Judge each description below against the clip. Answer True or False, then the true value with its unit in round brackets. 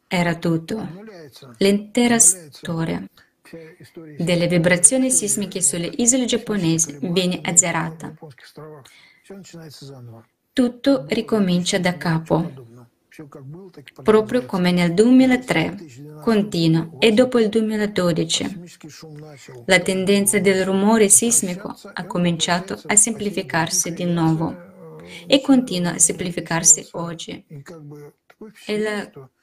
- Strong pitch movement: False (4.5 semitones)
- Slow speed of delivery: True (90 wpm)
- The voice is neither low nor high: True (175 Hz)